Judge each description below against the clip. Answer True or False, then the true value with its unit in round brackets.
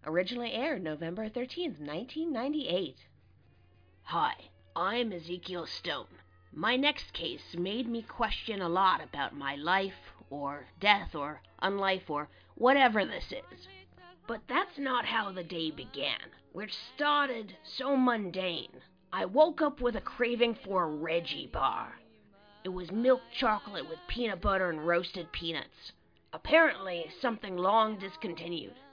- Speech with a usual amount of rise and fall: False (6.8 semitones)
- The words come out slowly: True (130 wpm)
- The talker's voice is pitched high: True (195 Hz)